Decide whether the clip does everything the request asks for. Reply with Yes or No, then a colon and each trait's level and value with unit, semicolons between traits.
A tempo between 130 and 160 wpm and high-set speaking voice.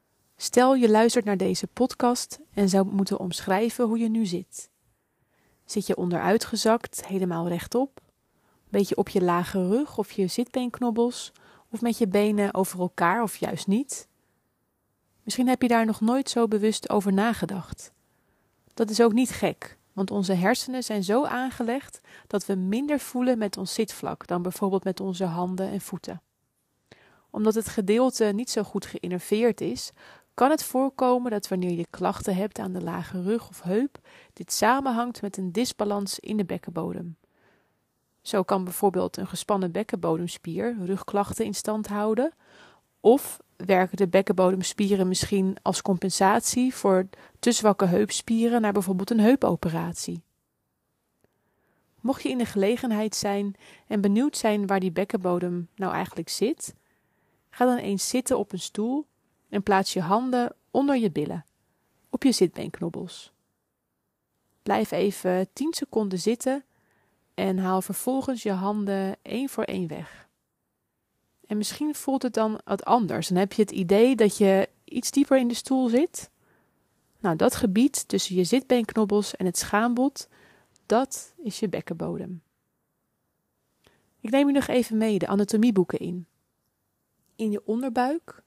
Yes: average, 145 wpm; high, 210 Hz